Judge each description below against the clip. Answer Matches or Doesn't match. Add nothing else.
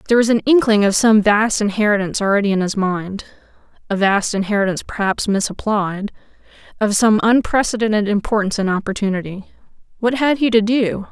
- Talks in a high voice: Matches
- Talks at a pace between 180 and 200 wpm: Doesn't match